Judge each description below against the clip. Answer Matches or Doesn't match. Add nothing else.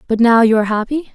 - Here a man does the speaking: Doesn't match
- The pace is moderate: Doesn't match